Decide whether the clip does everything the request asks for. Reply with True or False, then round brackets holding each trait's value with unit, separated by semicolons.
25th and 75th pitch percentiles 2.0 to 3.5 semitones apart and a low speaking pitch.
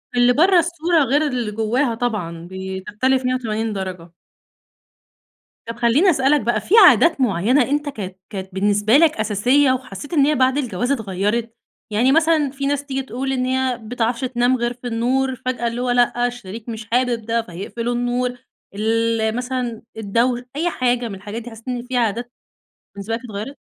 False (3.1 semitones; 245 Hz)